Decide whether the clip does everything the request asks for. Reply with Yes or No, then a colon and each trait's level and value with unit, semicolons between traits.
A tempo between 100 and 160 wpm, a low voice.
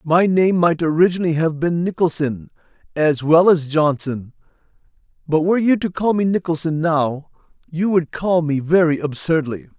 No: average, 155 wpm; medium, 160 Hz